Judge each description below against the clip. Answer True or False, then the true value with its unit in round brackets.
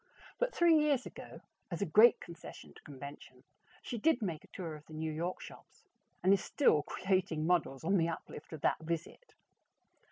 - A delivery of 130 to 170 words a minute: False (185 wpm)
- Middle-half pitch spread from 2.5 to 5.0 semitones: False (5.4 semitones)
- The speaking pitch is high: False (170 Hz)